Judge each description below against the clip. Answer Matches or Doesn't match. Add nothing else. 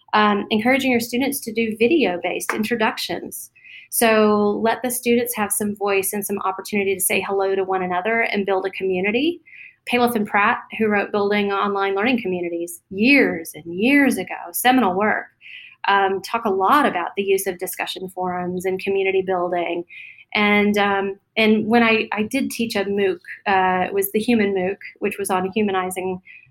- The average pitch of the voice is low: Doesn't match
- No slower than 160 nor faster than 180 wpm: Matches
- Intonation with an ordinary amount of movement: Matches